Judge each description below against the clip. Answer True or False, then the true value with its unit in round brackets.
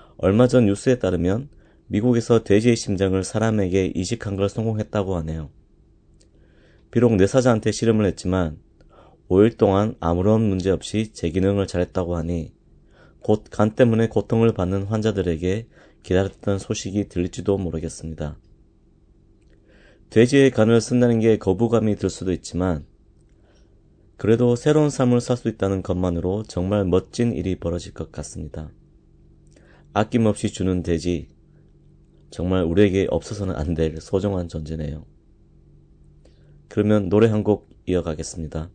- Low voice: True (95 Hz)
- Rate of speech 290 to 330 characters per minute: True (295 characters per minute)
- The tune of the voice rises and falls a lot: False (3.9 semitones)